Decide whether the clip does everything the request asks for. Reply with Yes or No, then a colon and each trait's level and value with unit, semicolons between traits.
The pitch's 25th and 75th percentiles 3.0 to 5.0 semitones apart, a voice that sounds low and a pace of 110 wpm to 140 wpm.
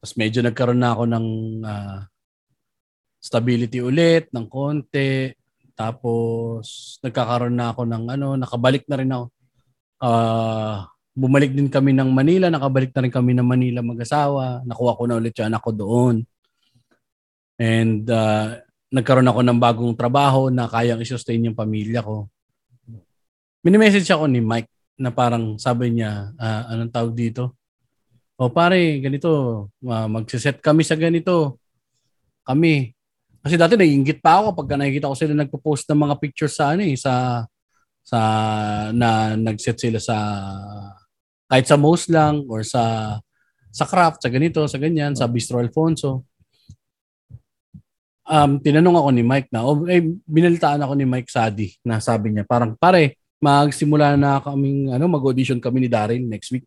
No: average, 3.6 semitones; low, 125 Hz; average, 150 wpm